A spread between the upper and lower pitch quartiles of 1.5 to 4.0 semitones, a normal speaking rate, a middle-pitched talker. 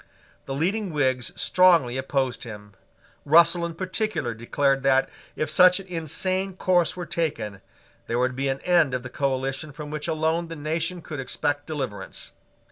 No: average, 4.4 semitones; average, 160 wpm; medium, 150 Hz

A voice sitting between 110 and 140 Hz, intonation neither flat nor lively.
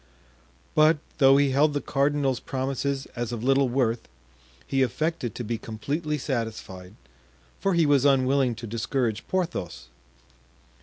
Yes: low, 135 Hz; average, 3.7 semitones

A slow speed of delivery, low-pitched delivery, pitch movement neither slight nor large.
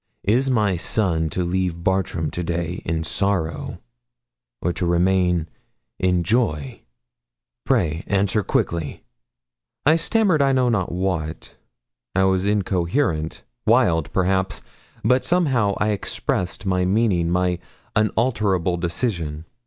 Yes: slow, 115 wpm; very low, 95 Hz; average, 3.8 semitones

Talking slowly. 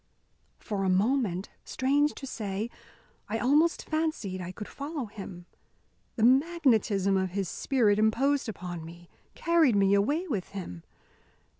Yes: slow, 130 wpm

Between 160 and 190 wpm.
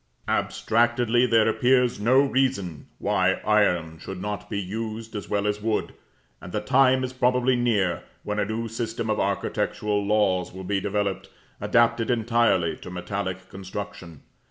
No: average, 150 wpm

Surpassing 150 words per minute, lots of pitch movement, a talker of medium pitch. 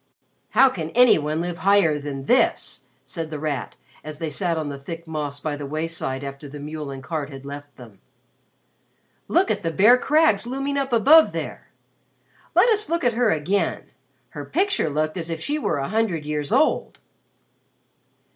Yes: average, 180 wpm; wide, 7.4 semitones; medium, 160 Hz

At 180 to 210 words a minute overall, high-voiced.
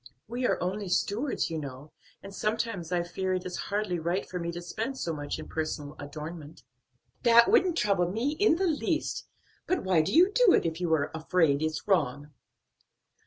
No: average, 190 wpm; medium, 180 Hz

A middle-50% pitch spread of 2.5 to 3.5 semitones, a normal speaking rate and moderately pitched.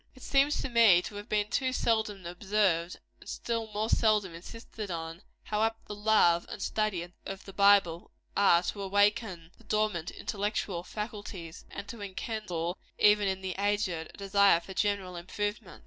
No: average, 3.1 semitones; average, 165 wpm; high, 205 Hz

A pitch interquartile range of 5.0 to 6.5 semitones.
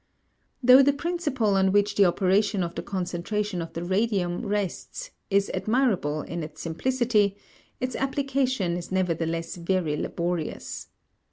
Yes: wide, 5.6 semitones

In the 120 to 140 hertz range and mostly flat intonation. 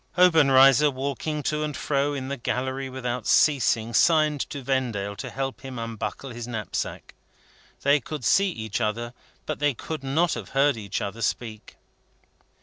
No: low, 135 Hz; average, 3.7 semitones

